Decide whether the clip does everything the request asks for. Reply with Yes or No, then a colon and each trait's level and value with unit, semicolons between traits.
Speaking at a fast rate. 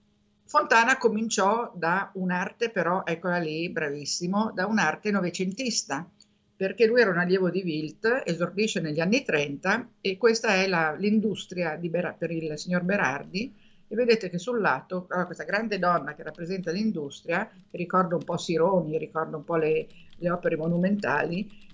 No: average, 150 wpm